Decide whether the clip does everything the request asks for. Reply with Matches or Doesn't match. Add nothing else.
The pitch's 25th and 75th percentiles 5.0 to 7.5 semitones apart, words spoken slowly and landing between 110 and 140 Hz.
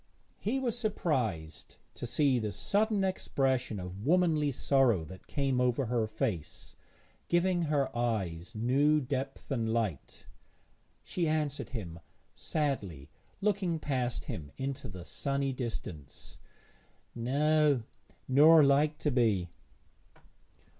Matches